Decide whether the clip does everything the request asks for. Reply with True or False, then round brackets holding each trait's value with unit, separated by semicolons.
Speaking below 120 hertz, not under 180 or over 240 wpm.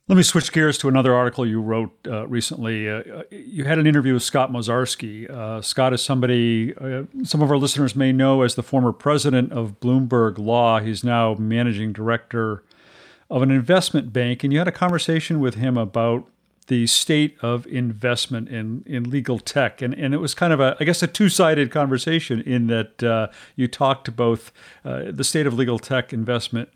False (125 Hz; 195 wpm)